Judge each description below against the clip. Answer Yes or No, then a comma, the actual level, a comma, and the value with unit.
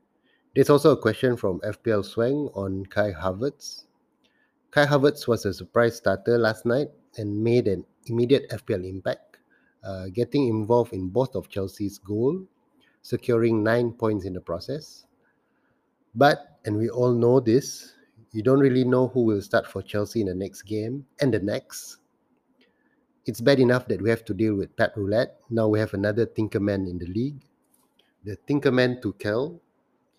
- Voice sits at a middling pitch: No, low, 115 Hz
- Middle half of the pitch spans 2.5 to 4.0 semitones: No, average, 4.4 semitones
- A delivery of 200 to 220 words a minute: No, average, 170 wpm